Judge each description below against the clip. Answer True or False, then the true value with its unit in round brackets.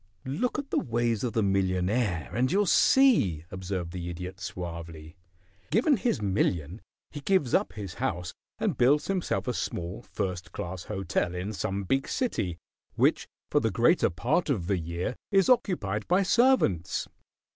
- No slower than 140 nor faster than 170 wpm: True (155 wpm)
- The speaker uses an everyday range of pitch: False (8.4 semitones)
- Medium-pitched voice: False (100 Hz)